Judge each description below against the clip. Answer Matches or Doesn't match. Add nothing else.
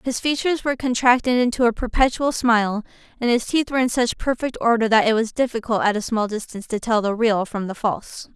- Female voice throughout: Matches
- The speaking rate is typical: Doesn't match